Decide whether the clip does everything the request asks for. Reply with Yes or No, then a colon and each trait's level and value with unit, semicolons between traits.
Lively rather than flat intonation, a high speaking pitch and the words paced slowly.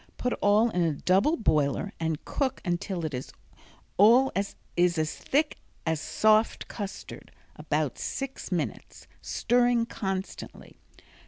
Yes: wide, 6.6 semitones; high, 195 Hz; slow, 115 wpm